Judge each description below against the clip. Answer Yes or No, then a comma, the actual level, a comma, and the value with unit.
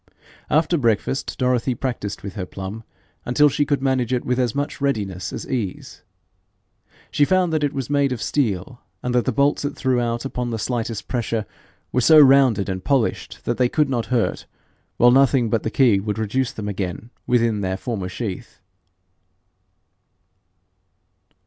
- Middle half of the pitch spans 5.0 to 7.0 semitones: No, average, 3.9 semitones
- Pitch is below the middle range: Yes, low, 120 Hz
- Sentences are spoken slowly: No, average, 170 wpm